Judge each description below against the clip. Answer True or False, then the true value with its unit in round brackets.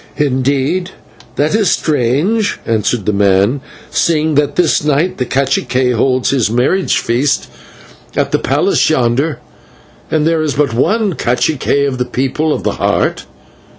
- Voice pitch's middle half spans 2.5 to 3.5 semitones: False (3.9 semitones)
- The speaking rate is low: False (145 wpm)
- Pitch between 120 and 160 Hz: True (140 Hz)